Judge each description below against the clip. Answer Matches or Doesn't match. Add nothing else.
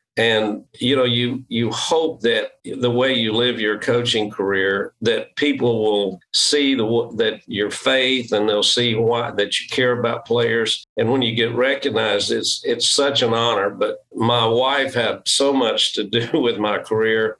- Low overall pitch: Matches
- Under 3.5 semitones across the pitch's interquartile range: Matches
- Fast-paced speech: Doesn't match